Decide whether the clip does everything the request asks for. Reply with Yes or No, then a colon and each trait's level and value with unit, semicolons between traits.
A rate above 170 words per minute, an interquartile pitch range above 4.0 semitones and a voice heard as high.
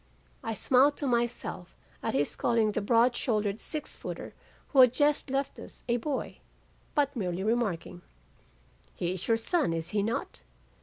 No: average, 160 wpm; average, 4.6 semitones; high, 230 Hz